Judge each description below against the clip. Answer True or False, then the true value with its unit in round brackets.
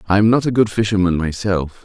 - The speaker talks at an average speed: False (230 wpm)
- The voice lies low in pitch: True (100 Hz)